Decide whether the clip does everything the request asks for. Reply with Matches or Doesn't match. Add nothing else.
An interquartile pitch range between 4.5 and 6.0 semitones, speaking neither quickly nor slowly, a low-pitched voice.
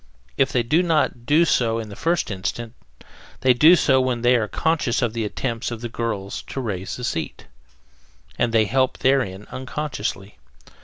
Doesn't match